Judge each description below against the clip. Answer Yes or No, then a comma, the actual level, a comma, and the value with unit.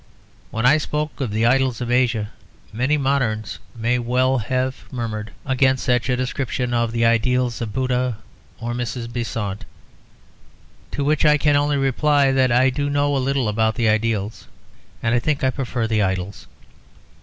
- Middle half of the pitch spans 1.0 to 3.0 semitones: Yes, average, 2.7 semitones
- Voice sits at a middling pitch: No, low, 125 Hz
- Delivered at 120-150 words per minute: No, average, 165 wpm